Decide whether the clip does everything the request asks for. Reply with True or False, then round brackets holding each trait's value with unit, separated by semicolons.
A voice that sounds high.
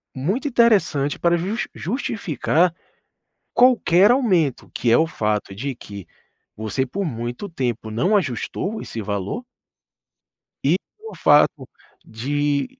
False (155 Hz)